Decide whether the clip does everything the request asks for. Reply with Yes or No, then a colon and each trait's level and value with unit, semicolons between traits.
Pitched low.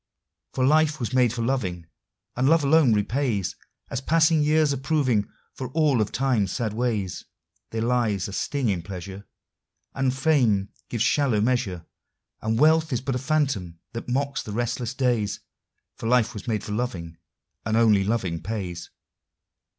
Yes: low, 120 Hz